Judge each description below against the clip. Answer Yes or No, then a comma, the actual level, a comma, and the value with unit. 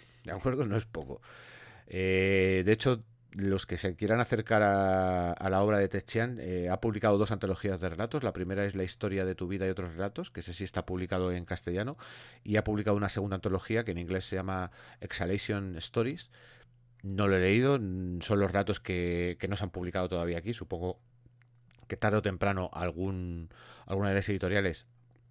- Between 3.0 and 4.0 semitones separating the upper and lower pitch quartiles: Yes, average, 3.3 semitones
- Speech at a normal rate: No, fast, 195 wpm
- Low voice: Yes, low, 100 Hz